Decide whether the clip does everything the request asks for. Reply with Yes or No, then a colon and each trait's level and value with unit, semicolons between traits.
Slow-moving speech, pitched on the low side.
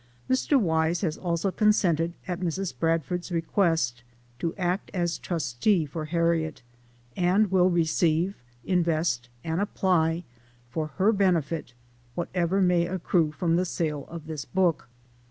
No: slow, 130 wpm; medium, 170 Hz